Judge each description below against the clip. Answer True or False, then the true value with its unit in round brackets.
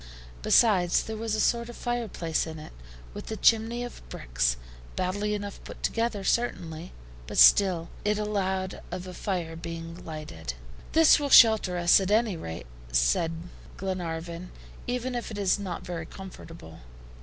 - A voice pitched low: False (185 Hz)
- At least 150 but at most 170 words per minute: True (155 wpm)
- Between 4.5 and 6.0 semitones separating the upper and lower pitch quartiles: True (4.8 semitones)